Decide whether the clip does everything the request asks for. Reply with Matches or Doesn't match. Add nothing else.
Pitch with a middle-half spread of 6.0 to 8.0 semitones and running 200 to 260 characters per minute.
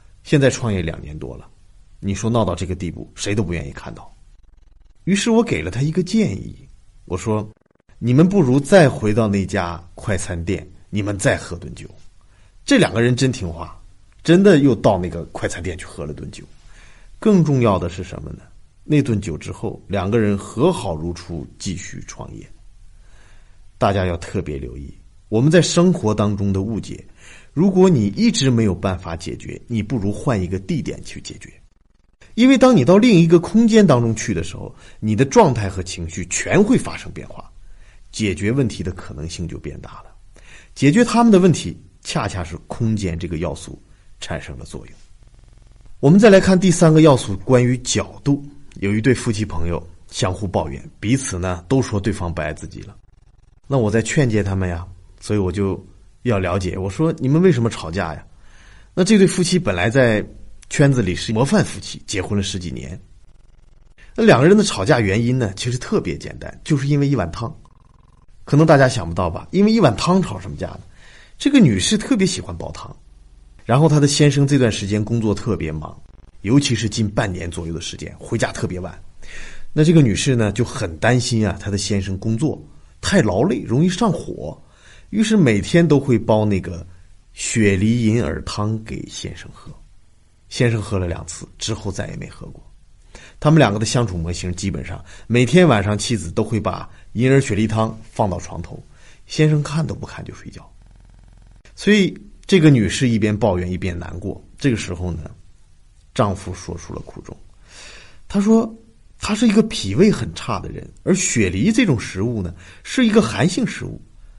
Doesn't match